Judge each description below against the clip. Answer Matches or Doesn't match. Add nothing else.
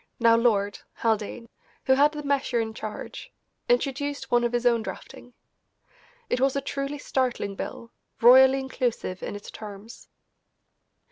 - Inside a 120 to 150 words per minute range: Matches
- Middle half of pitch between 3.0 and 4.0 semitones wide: Matches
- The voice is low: Doesn't match